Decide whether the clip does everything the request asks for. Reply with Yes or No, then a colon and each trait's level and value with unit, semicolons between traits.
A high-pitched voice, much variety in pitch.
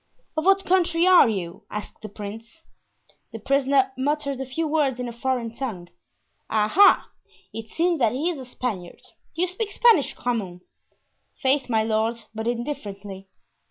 Yes: very high, 250 Hz; wide, 5.9 semitones